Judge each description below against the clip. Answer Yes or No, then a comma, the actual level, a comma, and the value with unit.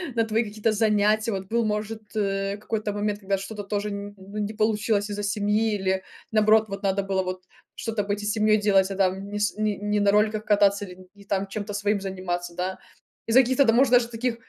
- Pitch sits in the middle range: No, high, 205 Hz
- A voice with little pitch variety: Yes, narrow, 1.5 semitones